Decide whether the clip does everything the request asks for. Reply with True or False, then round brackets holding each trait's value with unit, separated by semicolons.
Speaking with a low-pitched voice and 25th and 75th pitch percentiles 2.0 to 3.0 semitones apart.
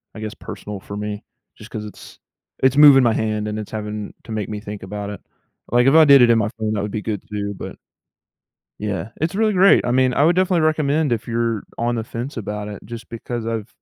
False (115 Hz; 4.0 semitones)